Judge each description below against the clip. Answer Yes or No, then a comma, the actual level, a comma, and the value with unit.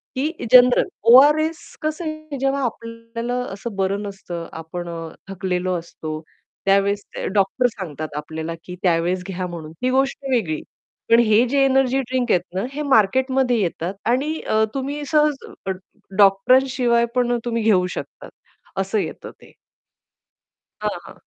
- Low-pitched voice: No, high, 230 Hz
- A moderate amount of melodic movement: No, wide, 6.0 semitones